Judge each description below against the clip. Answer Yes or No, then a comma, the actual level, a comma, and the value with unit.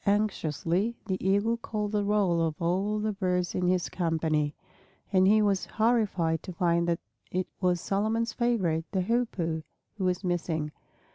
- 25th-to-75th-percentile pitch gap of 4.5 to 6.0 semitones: No, average, 3.7 semitones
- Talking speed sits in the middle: Yes, average, 155 wpm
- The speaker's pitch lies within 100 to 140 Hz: No, medium, 185 Hz